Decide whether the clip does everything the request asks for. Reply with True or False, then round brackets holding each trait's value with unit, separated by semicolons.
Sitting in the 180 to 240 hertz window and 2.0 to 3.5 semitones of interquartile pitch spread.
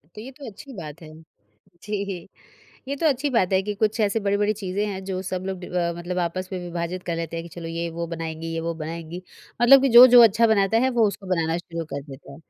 False (185 Hz; 4.3 semitones)